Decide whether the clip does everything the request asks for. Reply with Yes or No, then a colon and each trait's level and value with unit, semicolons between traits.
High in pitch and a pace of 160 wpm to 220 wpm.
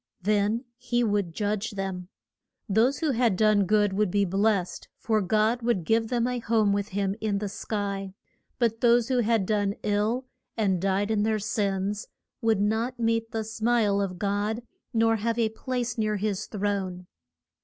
Yes: high, 215 Hz; average, 170 wpm